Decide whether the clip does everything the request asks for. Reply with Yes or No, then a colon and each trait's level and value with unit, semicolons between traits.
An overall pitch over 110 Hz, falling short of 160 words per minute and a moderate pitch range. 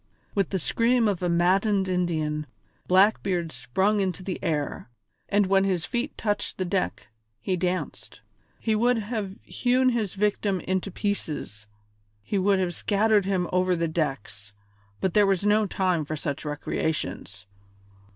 Yes: high, 190 Hz; average, 150 wpm; average, 3.7 semitones